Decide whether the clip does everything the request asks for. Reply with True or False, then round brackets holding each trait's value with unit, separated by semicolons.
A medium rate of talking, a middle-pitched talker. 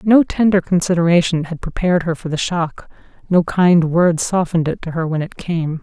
True (195 wpm; 170 Hz)